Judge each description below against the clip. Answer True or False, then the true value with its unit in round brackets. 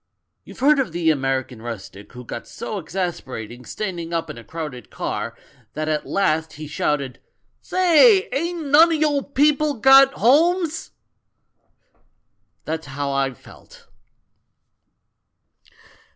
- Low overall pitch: False (165 Hz)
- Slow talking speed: True (125 wpm)